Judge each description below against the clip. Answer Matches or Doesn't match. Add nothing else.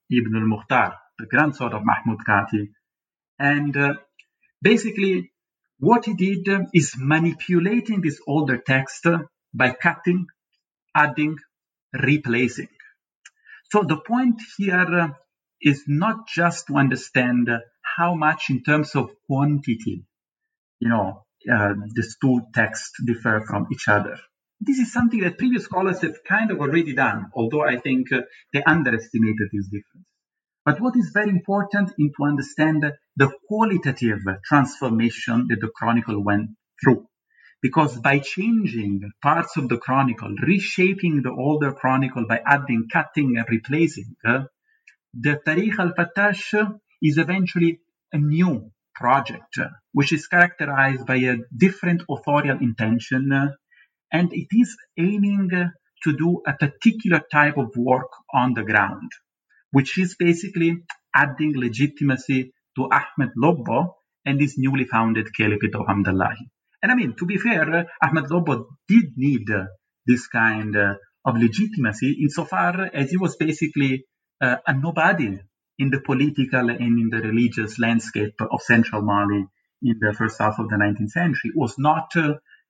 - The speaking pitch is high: Doesn't match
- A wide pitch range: Matches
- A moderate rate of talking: Matches